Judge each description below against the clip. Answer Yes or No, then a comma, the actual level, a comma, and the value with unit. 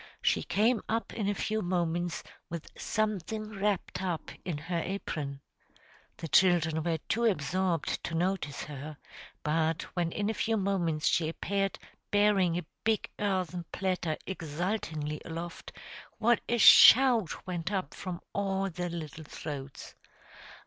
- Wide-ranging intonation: No, average, 3.8 semitones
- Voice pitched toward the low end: No, medium, 180 Hz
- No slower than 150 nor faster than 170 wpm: No, slow, 135 wpm